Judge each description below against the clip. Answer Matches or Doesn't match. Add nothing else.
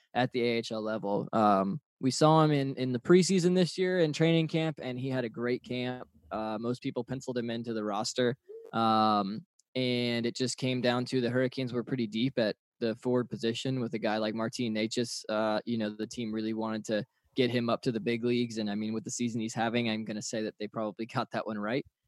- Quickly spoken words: Matches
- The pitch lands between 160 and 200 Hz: Doesn't match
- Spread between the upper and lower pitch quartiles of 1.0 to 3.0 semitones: Matches